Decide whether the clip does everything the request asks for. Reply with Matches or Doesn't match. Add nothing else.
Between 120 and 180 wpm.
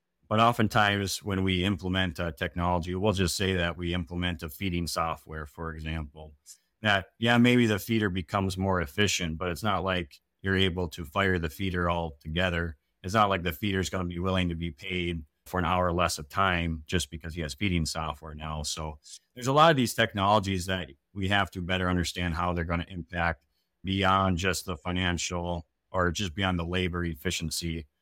Doesn't match